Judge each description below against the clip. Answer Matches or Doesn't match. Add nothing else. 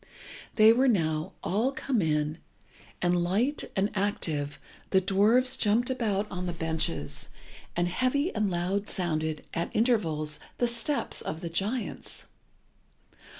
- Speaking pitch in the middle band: Doesn't match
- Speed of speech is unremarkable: Doesn't match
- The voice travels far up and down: Matches